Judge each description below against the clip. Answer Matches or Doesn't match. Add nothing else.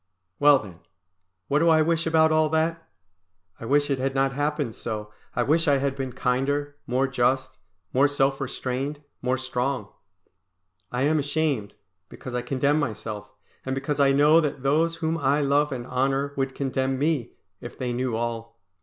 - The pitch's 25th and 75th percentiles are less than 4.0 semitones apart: Matches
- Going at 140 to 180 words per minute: Matches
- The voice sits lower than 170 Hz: Matches